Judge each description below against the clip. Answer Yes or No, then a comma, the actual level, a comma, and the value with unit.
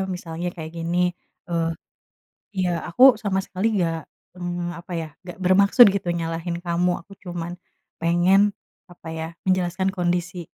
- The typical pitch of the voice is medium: Yes, medium, 175 Hz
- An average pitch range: No, narrow, 1.6 semitones